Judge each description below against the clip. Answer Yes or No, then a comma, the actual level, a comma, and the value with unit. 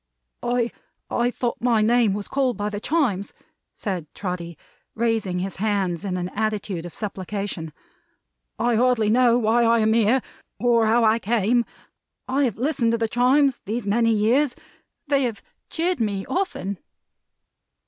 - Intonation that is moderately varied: Yes, average, 3.2 semitones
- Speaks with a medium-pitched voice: No, high, 225 Hz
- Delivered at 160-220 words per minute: No, average, 150 wpm